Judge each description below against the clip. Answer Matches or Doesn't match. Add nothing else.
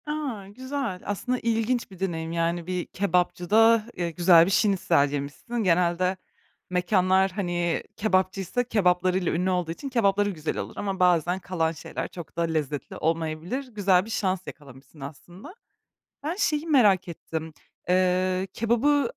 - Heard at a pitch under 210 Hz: Matches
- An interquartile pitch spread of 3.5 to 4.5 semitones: Matches